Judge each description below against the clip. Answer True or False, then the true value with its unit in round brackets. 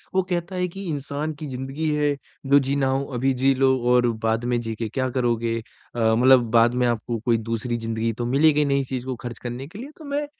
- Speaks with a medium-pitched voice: False (130 Hz)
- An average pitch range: True (3.2 semitones)